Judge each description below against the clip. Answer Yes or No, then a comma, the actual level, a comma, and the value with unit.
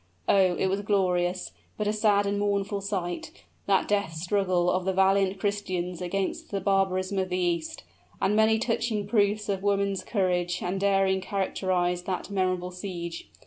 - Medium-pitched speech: No, high, 195 Hz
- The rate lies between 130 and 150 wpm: No, average, 165 wpm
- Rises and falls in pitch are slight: Yes, narrow, 1.9 semitones